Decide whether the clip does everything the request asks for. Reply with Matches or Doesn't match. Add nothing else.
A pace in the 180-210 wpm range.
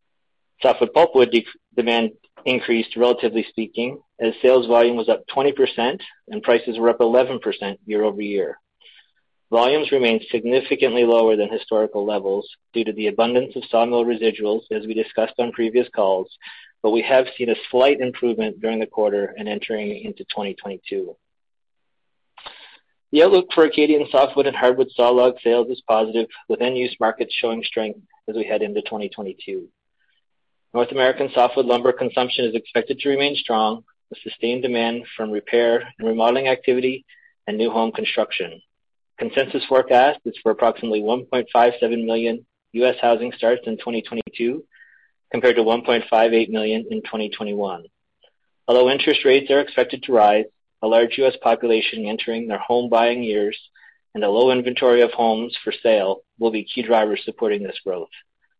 Doesn't match